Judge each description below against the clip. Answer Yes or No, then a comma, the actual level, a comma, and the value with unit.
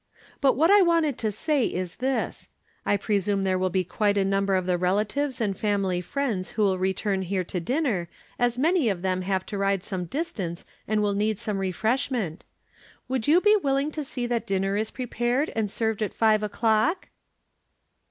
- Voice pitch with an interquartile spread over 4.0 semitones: Yes, average, 5.0 semitones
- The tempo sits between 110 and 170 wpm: No, average, 190 wpm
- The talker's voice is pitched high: Yes, high, 210 Hz